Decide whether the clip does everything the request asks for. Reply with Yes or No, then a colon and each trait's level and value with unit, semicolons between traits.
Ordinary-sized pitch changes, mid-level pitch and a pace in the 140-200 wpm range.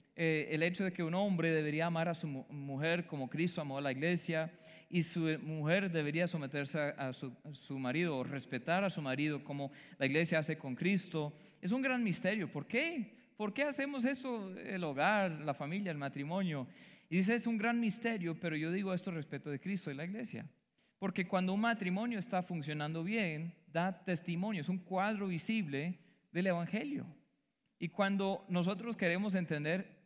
Yes: average, 4.1 semitones; medium, 175 Hz; average, 185 wpm